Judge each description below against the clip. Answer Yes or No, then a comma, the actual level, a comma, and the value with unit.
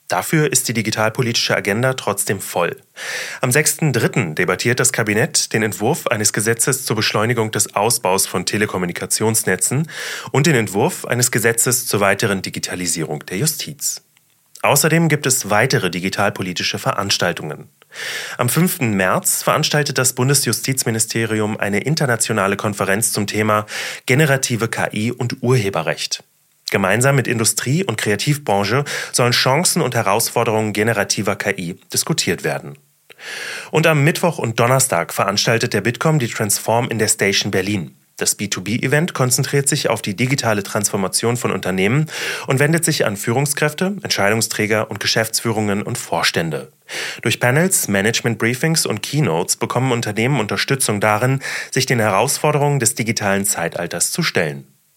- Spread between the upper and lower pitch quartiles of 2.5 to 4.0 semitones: No, average, 4.4 semitones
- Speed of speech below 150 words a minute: Yes, average, 130 wpm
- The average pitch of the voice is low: Yes, low, 115 Hz